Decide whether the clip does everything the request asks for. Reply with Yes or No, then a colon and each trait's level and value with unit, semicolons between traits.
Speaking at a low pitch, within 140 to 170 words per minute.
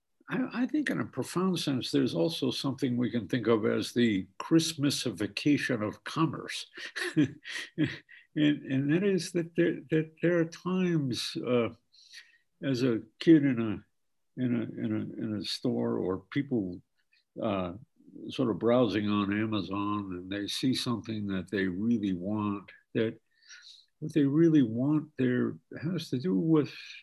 Yes: low, 125 Hz; average, 150 wpm